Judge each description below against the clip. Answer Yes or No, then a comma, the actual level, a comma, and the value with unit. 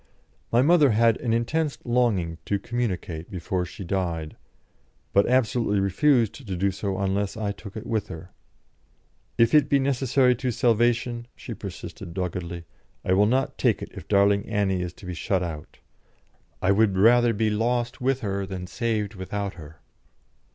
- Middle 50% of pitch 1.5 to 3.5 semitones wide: No, average, 4.2 semitones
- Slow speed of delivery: No, average, 165 wpm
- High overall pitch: No, low, 105 Hz